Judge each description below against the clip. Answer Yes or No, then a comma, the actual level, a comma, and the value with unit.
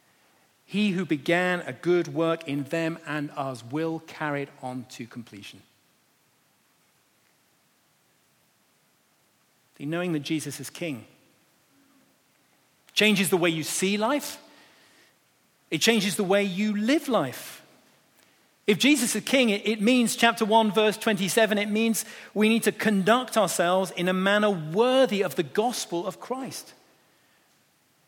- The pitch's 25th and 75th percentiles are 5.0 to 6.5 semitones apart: Yes, average, 5.3 semitones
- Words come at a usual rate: No, slow, 130 wpm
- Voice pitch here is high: Yes, high, 195 Hz